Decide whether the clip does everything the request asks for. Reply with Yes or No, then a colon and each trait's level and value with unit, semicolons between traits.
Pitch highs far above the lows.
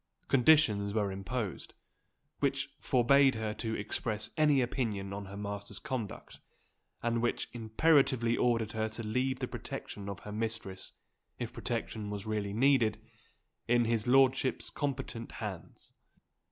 No: average, 3.7 semitones